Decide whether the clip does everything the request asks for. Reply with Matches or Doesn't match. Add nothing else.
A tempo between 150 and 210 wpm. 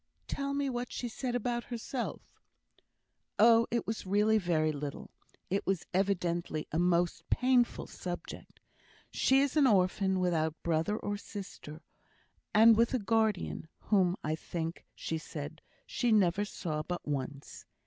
Doesn't match